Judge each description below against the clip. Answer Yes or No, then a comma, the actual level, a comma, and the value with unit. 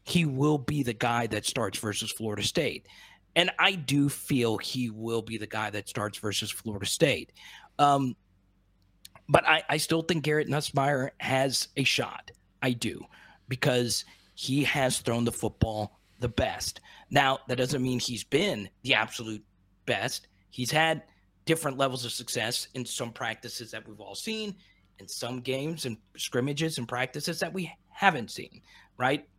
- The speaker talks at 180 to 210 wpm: No, average, 160 wpm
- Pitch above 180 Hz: No, low, 120 Hz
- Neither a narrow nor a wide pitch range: Yes, average, 4.7 semitones